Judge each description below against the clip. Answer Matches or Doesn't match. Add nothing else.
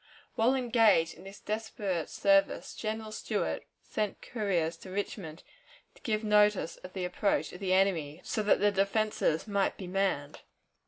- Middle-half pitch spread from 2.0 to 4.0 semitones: Matches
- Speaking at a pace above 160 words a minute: Doesn't match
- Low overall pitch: Doesn't match